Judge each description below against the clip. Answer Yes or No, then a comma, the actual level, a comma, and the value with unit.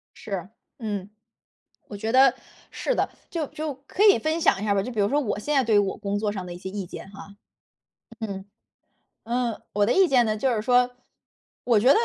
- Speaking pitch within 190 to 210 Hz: No, high, 220 Hz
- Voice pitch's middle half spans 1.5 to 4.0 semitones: No, average, 4.5 semitones